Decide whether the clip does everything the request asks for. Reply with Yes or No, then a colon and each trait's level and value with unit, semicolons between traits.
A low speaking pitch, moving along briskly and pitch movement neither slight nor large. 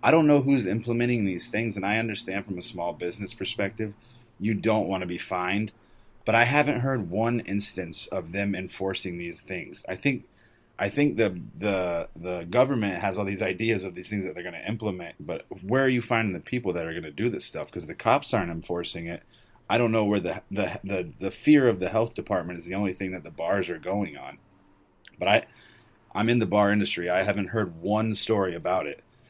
Yes: low, 105 Hz; fast, 225 wpm; average, 3.7 semitones